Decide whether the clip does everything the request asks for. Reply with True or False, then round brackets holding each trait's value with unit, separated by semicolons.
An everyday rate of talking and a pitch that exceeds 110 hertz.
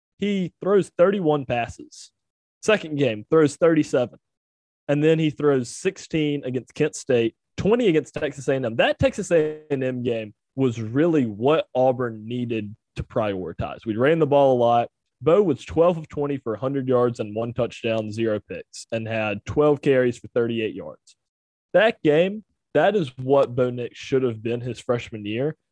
True (165 wpm; 135 Hz)